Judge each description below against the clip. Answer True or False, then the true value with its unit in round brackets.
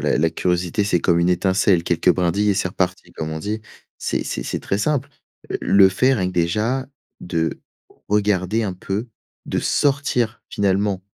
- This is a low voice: True (95 Hz)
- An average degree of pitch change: True (3.0 semitones)